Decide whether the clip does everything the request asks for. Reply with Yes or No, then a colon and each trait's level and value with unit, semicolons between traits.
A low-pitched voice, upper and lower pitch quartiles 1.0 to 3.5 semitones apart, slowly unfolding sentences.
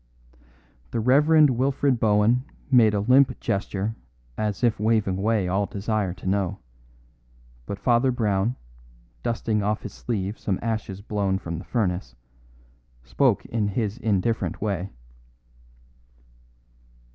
Yes: low, 105 Hz; average, 3.1 semitones; slow, 120 wpm